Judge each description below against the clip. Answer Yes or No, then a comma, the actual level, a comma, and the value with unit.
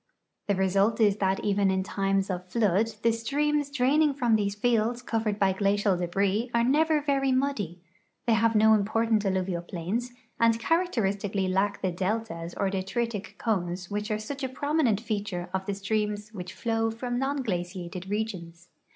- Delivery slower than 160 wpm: No, average, 165 wpm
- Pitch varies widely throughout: No, average, 3.6 semitones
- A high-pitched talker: Yes, high, 210 Hz